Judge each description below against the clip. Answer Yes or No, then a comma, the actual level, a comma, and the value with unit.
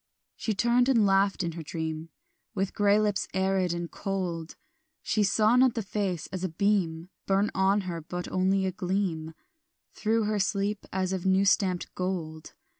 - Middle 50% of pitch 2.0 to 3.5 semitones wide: Yes, average, 2.7 semitones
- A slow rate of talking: No, average, 170 wpm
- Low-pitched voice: No, high, 190 Hz